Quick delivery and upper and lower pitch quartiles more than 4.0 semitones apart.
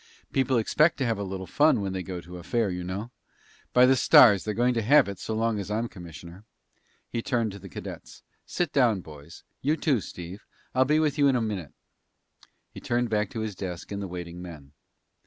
Yes: fast, 220 wpm; average, 5.2 semitones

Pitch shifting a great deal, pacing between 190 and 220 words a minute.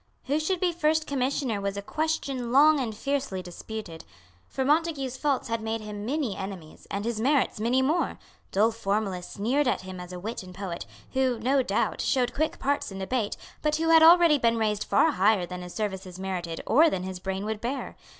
Yes: wide, 6.4 semitones; average, 200 wpm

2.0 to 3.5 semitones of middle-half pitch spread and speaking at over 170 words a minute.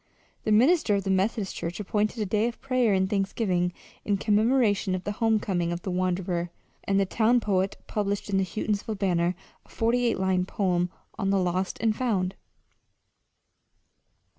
No: average, 2.8 semitones; average, 165 wpm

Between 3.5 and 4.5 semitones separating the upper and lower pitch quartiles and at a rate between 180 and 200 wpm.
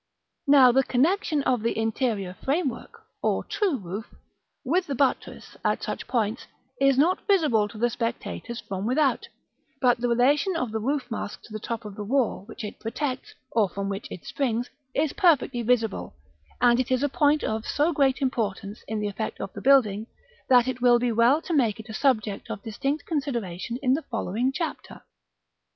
Yes: average, 4.1 semitones; average, 190 wpm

